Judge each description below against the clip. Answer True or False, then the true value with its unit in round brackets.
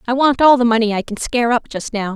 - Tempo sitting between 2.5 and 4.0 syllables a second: False (6.7 syllables/s)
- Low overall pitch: False (235 Hz)